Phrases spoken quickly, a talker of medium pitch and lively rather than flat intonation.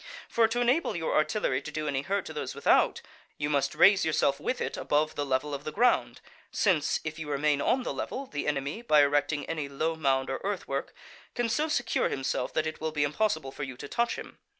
Yes: fast, 225 wpm; medium, 155 Hz; wide, 5.9 semitones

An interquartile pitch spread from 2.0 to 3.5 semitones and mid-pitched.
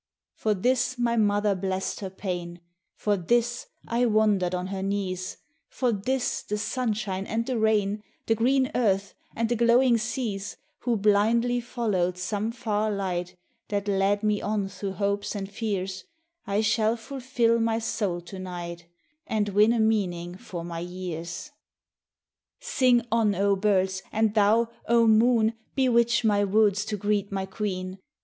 No: average, 3.2 semitones; high, 210 Hz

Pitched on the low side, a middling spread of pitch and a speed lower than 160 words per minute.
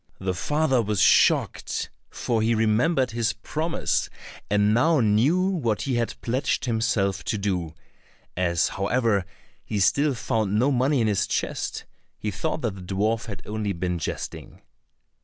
Yes: low, 110 Hz; average, 4.2 semitones; average, 145 wpm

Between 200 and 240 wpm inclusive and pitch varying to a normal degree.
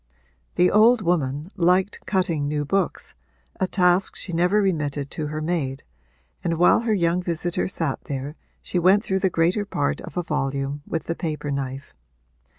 No: average, 165 wpm; average, 4.2 semitones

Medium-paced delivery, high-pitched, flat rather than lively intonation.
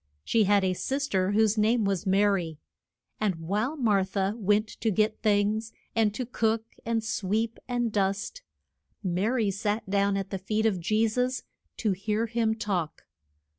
Yes: average, 170 wpm; high, 210 Hz; narrow, 2.3 semitones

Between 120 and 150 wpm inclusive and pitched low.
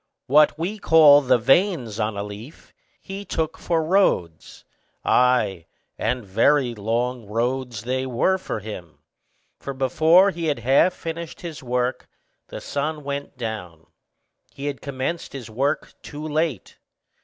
Yes: average, 140 wpm; low, 130 Hz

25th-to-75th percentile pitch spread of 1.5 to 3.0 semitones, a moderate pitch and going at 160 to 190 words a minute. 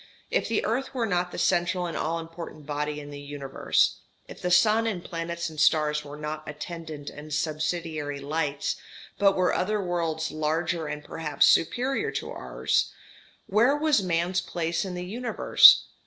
No: average, 3.4 semitones; medium, 165 Hz; average, 165 wpm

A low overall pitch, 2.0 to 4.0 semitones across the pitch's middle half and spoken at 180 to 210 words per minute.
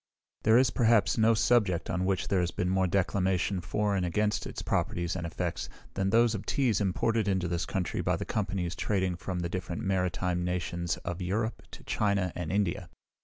Yes: very low, 95 Hz; average, 2.9 semitones; average, 190 wpm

